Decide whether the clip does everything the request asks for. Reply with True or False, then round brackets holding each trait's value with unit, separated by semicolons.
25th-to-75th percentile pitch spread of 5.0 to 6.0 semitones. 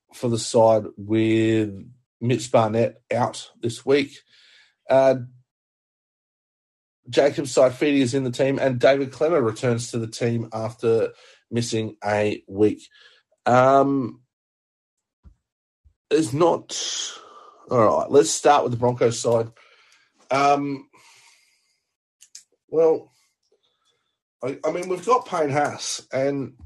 True (5.4 semitones)